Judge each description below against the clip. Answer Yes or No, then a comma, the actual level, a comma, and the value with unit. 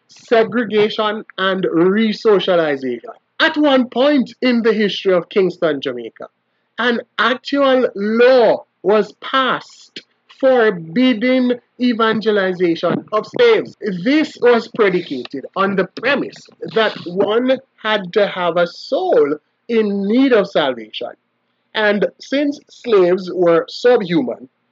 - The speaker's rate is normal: No, slow, 105 wpm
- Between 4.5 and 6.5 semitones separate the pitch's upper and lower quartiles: Yes, average, 4.8 semitones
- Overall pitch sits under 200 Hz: No, high, 215 Hz